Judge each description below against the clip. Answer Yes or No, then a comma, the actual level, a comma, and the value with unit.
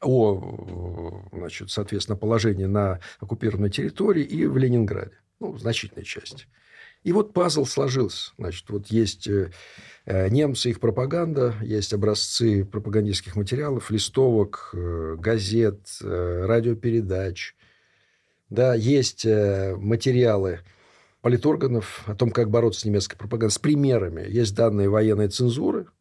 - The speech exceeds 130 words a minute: No, slow, 110 wpm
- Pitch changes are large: No, average, 3.3 semitones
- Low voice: Yes, low, 110 Hz